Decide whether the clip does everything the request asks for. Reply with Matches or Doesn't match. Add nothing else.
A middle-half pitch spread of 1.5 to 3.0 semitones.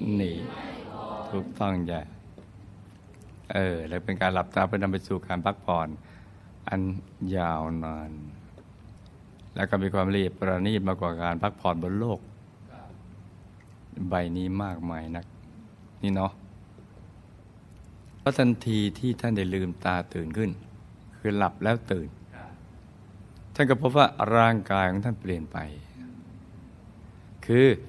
Matches